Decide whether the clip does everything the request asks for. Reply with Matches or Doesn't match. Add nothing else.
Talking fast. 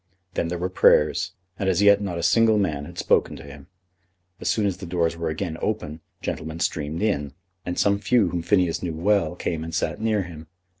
Matches